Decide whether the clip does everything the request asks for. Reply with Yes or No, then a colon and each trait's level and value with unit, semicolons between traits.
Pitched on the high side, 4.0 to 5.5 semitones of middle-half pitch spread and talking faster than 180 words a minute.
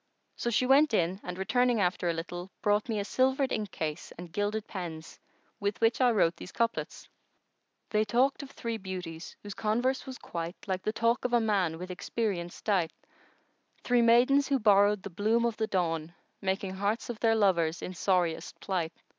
Yes: high, 205 Hz; average, 4.6 semitones; average, 190 wpm